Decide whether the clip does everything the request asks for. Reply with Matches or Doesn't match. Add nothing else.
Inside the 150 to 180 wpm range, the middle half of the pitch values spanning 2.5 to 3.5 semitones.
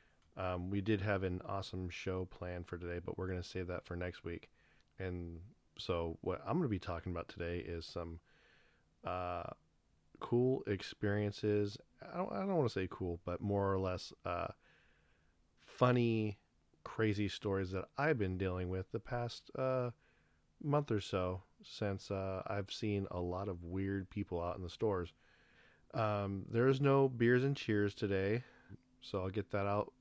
Matches